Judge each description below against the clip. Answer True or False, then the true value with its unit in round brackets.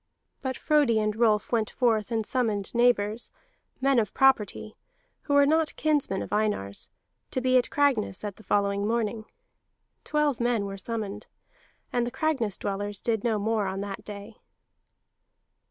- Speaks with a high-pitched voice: True (220 Hz)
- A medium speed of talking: True (155 wpm)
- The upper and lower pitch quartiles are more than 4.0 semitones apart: False (3.7 semitones)